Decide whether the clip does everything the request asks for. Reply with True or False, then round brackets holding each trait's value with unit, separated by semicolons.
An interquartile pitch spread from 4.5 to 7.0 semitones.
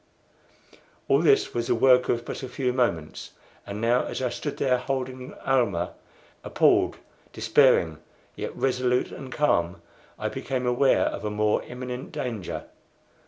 False (2.8 semitones)